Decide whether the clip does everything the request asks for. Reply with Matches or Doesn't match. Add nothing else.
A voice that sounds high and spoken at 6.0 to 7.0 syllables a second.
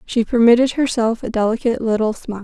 Matches